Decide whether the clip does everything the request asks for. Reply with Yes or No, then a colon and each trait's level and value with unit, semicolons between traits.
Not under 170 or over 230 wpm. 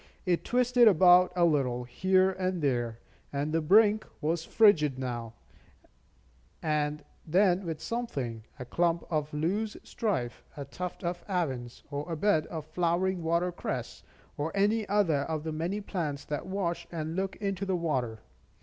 No: average, 150 wpm